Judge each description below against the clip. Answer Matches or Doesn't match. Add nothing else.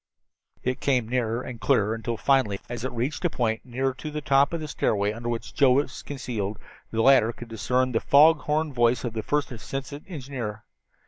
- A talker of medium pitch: Doesn't match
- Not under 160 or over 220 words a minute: Matches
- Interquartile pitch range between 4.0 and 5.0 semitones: Doesn't match